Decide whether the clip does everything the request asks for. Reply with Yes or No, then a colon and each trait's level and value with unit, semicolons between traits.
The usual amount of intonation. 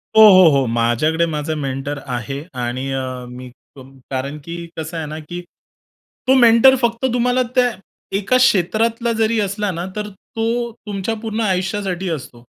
No: wide, 8.3 semitones